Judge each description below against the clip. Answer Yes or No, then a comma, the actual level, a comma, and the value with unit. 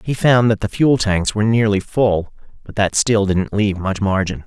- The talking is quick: Yes, fast, 215 wpm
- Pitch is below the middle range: Yes, low, 105 Hz